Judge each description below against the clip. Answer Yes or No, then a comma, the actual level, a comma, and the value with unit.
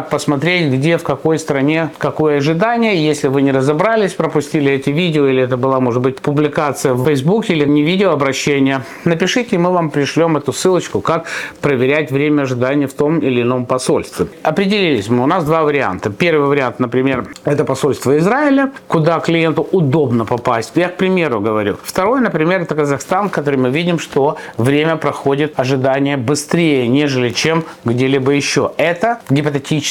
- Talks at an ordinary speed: No, fast, 165 wpm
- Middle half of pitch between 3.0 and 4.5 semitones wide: Yes, average, 3.6 semitones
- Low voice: No, medium, 150 Hz